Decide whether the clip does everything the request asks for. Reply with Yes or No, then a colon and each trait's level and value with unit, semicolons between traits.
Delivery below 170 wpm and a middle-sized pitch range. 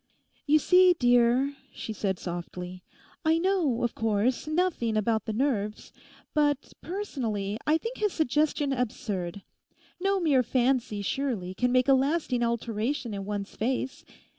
No: average, 140 wpm; wide, 5.7 semitones